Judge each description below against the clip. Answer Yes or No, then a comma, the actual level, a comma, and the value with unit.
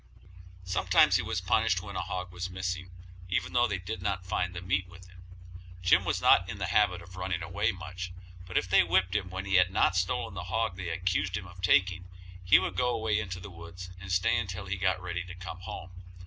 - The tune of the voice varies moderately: No, narrow, 1.0 semitones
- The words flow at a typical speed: No, fast, 230 wpm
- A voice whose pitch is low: Yes, very low, 90 Hz